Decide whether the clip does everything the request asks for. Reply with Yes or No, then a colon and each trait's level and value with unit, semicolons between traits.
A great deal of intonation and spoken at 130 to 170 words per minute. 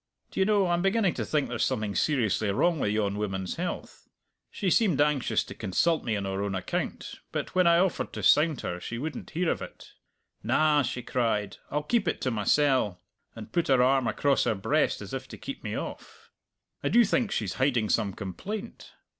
No: wide, 8.4 semitones; average, 200 wpm